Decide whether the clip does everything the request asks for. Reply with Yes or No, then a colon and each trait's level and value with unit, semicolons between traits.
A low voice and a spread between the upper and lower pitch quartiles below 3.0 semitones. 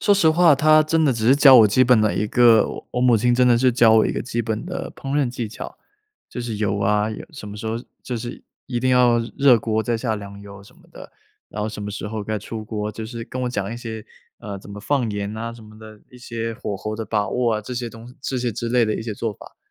Yes: low, 115 Hz; narrow, 2.6 semitones